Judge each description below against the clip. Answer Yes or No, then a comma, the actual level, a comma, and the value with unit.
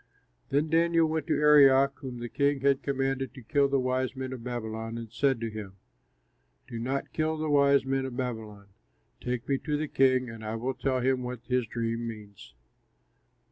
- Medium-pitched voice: No, low, 130 Hz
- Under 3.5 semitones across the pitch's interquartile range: Yes, average, 3.1 semitones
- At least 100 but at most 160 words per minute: No, average, 190 wpm